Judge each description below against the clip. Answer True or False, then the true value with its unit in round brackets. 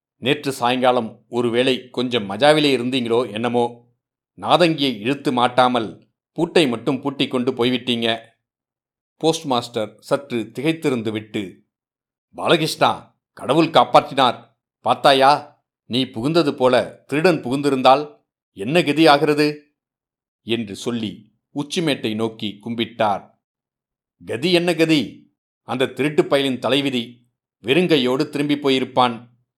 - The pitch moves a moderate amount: True (3.3 semitones)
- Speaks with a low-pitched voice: True (130 Hz)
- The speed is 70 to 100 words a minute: True (95 wpm)